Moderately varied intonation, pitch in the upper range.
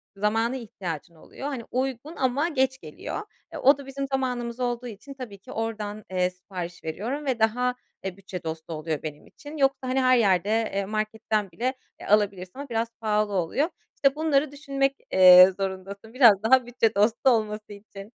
Yes: average, 5.0 semitones; high, 225 Hz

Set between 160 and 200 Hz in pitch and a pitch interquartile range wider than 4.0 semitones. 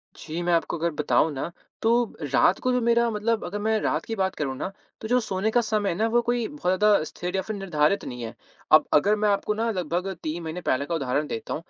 Yes: high, 190 Hz; wide, 5.5 semitones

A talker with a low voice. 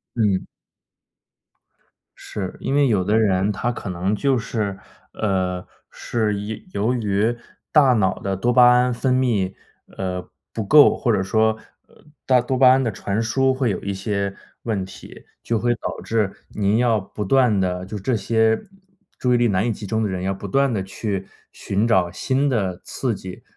Yes: low, 110 Hz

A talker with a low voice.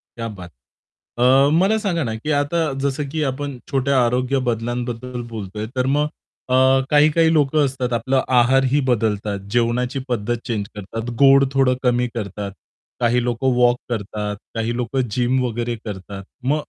Yes: low, 125 Hz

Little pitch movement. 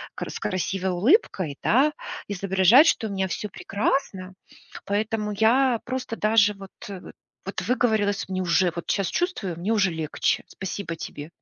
No: average, 3.1 semitones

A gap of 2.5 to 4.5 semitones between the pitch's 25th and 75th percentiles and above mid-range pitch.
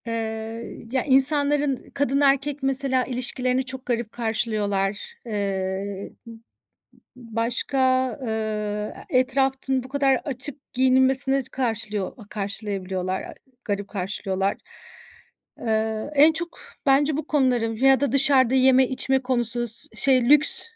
Yes: average, 3.6 semitones; very high, 250 Hz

